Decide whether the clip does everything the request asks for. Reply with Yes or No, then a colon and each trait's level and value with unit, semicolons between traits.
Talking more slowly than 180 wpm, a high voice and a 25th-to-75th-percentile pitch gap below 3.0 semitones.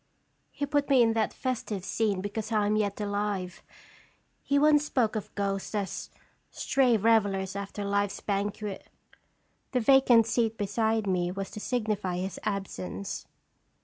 Yes: average, 145 wpm; high, 210 Hz; narrow, 2.5 semitones